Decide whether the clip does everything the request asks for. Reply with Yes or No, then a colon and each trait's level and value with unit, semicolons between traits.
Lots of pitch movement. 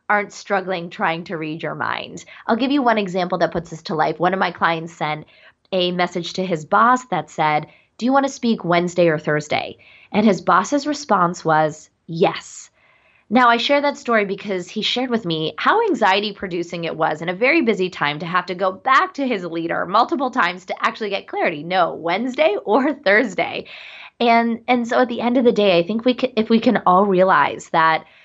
Yes: wide, 5.7 semitones